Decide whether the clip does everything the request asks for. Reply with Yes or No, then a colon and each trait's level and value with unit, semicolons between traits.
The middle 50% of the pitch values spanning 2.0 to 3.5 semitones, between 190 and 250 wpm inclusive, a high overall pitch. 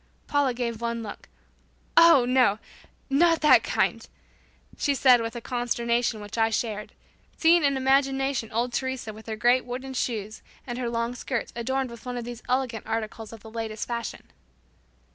No: narrow, 2.6 semitones; average, 165 wpm; high, 240 Hz